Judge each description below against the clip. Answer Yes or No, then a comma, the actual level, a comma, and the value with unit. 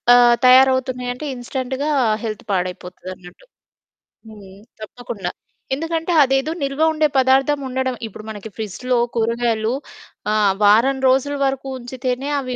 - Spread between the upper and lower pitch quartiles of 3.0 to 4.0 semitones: Yes, average, 3.5 semitones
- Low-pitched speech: No, very high, 250 Hz